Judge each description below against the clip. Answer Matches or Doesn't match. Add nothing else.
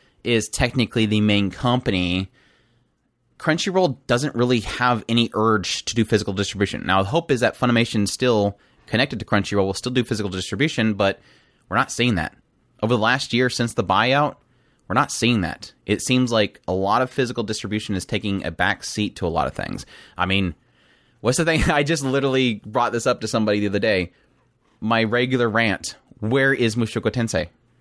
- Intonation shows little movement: Doesn't match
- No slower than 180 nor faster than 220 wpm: Matches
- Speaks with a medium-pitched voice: Doesn't match